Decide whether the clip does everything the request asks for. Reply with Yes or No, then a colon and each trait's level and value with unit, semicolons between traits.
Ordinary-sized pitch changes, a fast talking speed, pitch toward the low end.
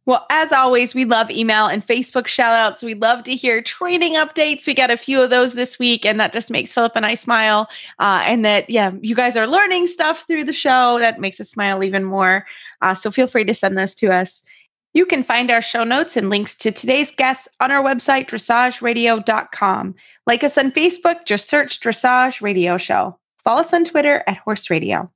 No: average, 3.9 semitones; fast, 215 wpm; high, 235 Hz